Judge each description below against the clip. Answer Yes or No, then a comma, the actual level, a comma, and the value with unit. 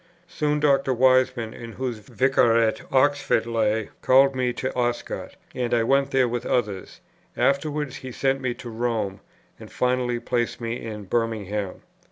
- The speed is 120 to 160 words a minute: Yes, average, 150 wpm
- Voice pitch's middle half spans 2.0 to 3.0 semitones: Yes, narrow, 2.5 semitones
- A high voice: No, low, 120 Hz